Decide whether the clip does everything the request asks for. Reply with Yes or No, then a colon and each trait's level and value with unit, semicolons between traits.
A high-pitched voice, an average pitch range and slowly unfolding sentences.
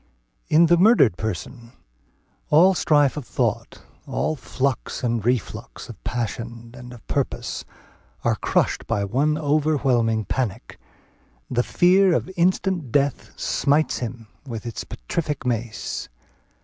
No: low, 130 Hz; average, 4.8 semitones; slow, 125 wpm